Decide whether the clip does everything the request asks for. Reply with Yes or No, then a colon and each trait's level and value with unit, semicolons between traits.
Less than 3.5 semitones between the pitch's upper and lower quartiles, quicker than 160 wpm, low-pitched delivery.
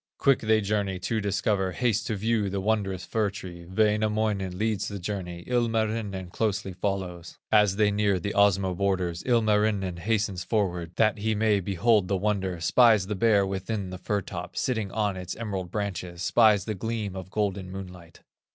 Yes: narrow, 2.6 semitones; average, 170 wpm; low, 100 Hz